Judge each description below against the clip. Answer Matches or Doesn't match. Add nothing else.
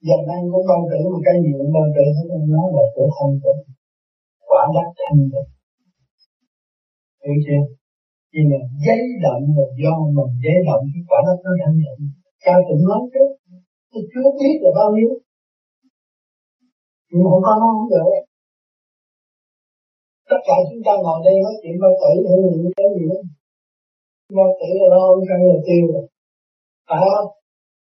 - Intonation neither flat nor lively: Doesn't match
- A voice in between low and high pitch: Matches